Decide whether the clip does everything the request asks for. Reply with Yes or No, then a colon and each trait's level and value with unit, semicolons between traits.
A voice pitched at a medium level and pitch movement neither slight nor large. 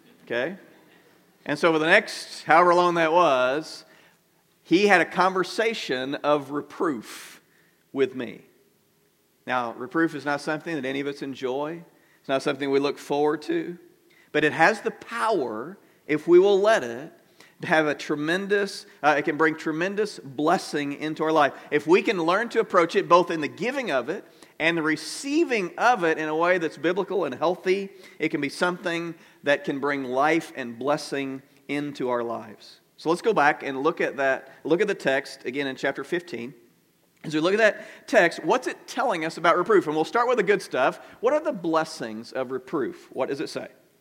Yes: medium, 155 Hz; average, 3.8 semitones